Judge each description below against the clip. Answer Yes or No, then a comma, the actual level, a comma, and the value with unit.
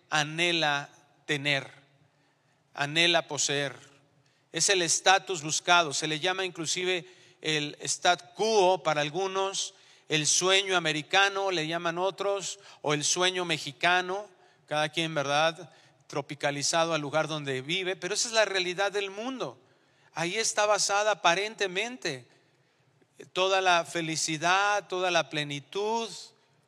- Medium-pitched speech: Yes, medium, 165 Hz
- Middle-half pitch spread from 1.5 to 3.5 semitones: No, average, 4.4 semitones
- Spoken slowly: Yes, slow, 120 wpm